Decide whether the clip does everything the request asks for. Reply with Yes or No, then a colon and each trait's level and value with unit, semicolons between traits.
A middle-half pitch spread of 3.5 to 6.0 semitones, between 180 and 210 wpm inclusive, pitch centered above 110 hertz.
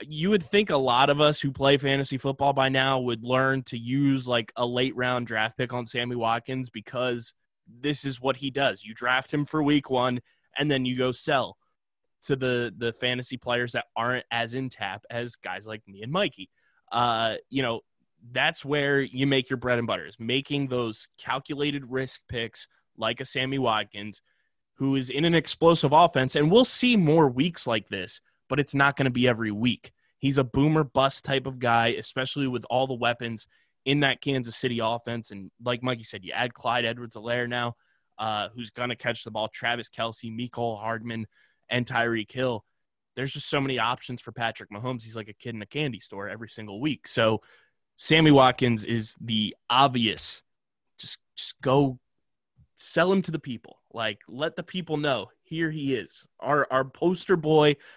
No: average, 3.0 semitones; average, 195 wpm; low, 125 Hz